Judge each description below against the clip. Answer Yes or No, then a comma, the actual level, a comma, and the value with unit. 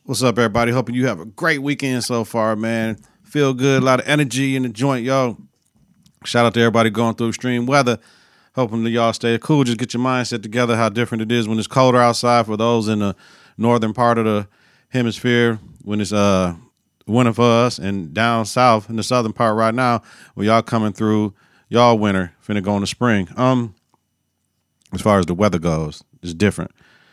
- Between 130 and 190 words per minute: No, fast, 205 wpm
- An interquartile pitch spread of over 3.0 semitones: No, narrow, 2.6 semitones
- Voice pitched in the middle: No, low, 115 Hz